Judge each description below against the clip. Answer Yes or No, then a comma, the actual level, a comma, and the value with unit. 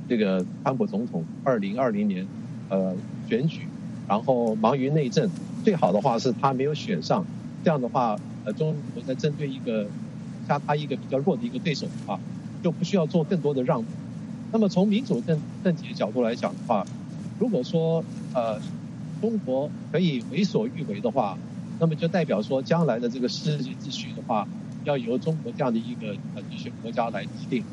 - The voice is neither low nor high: Yes, medium, 165 Hz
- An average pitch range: No, wide, 6.5 semitones